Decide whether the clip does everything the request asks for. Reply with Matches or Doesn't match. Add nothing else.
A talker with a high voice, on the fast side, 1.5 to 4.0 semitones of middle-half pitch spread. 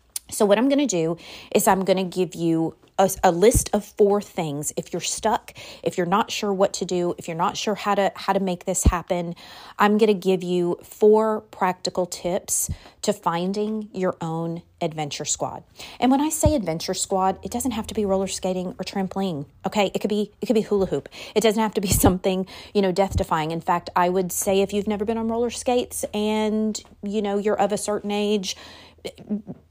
Matches